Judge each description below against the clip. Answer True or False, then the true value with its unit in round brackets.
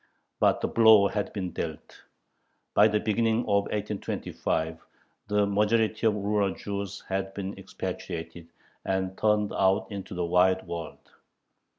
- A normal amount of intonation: False (2.0 semitones)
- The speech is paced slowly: True (130 wpm)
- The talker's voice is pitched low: True (100 Hz)